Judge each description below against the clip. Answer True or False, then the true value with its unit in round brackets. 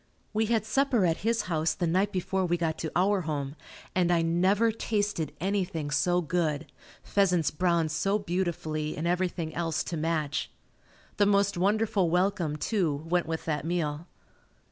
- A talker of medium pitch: True (175 Hz)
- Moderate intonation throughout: True (3.8 semitones)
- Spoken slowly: False (160 wpm)